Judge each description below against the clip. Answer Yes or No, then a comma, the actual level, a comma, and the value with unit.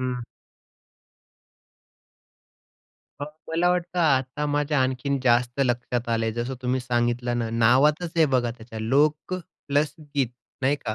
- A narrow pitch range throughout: No, average, 3.5 semitones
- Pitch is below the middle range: Yes, low, 130 Hz